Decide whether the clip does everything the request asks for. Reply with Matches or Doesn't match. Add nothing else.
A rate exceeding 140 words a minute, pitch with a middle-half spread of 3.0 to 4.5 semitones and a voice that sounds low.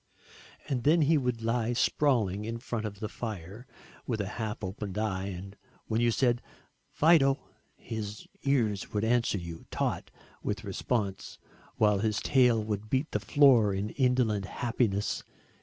Matches